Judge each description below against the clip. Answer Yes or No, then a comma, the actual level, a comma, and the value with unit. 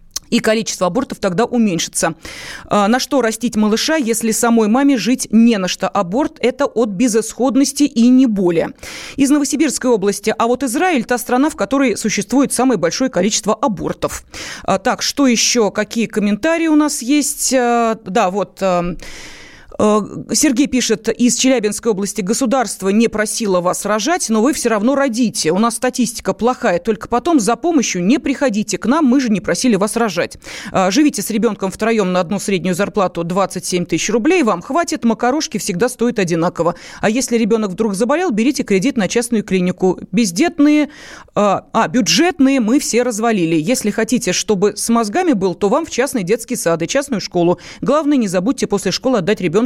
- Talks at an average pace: No, fast, 165 wpm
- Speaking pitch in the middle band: No, high, 230 Hz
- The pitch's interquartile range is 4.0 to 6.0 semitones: Yes, average, 4.3 semitones